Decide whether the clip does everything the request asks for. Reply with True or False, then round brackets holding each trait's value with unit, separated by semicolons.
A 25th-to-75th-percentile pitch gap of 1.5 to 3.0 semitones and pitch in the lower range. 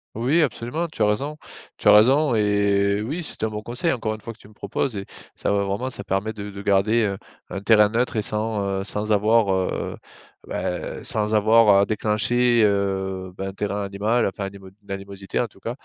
True (2.5 semitones; 105 Hz)